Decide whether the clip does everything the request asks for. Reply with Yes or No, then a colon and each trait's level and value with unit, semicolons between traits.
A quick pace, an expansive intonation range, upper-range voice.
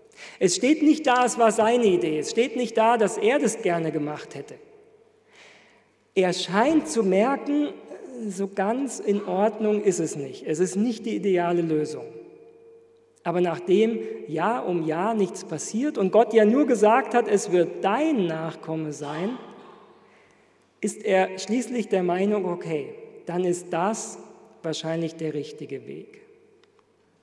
No: average, 145 wpm; wide, 7.4 semitones; high, 210 Hz